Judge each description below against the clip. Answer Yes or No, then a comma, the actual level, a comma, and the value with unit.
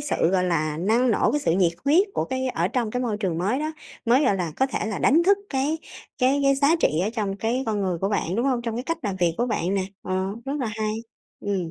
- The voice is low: No, high, 220 Hz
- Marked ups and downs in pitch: Yes, wide, 5.8 semitones